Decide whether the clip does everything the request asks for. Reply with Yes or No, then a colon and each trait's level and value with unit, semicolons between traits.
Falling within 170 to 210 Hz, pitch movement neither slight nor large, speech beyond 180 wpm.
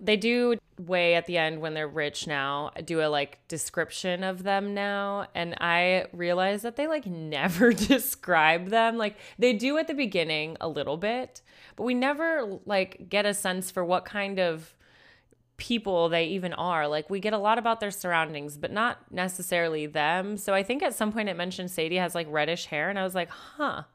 Yes: medium, 185 Hz; average, 4.3 semitones; average, 200 wpm